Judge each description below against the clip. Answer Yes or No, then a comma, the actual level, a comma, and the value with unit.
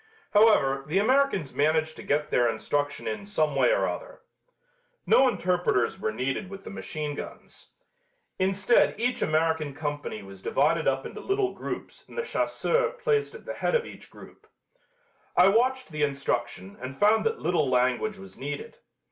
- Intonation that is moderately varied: No, wide, 8.0 semitones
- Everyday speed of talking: Yes, average, 165 wpm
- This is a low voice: No, medium, 160 Hz